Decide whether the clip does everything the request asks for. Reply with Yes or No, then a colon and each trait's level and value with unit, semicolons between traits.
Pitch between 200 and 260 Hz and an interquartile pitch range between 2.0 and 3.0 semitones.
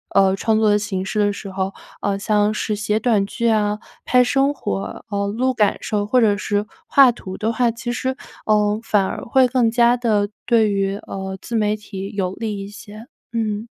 Yes: high, 210 Hz; narrow, 2.4 semitones